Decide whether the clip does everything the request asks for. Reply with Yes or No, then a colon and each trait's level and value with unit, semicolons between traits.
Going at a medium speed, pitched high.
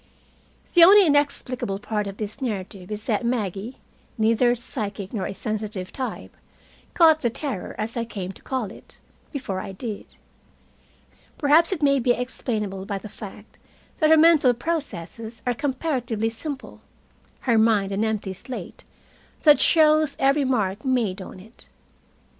Yes: average, 150 wpm; high, 230 Hz